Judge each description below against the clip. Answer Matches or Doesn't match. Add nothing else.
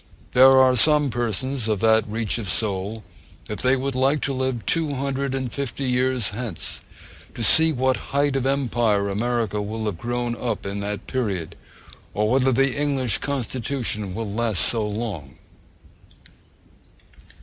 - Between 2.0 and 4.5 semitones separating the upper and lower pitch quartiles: Matches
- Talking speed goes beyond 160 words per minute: Doesn't match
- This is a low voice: Matches